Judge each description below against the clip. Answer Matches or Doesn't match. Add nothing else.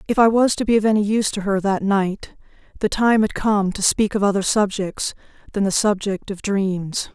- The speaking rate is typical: Doesn't match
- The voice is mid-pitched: Doesn't match